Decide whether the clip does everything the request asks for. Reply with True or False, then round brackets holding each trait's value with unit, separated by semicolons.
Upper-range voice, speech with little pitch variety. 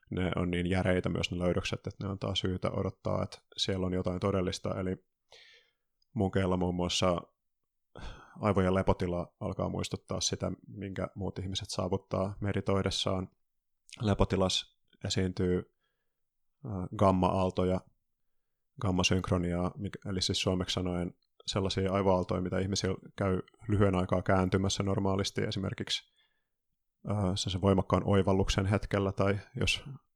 False (95 Hz; 1.2 semitones)